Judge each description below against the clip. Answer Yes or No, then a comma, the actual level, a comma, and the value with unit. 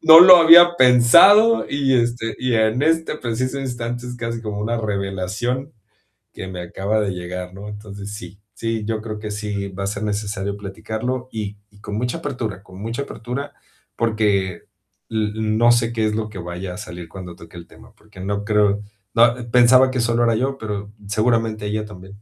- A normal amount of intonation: Yes, average, 3.2 semitones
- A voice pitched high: No, low, 110 Hz